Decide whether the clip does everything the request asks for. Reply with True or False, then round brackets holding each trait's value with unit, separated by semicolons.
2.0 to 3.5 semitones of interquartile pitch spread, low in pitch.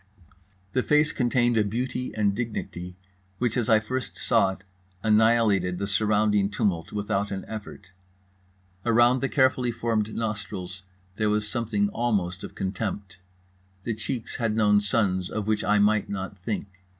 True (2.7 semitones; 105 Hz)